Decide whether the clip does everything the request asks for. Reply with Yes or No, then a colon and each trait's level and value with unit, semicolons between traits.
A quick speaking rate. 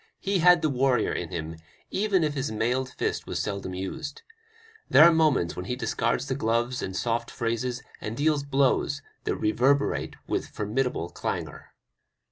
No: average, 155 wpm